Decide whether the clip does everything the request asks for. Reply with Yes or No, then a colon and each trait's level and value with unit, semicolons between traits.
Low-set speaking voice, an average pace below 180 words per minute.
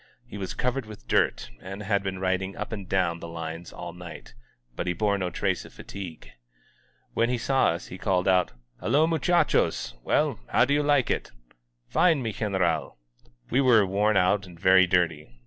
No: very low, 95 Hz; average, 185 wpm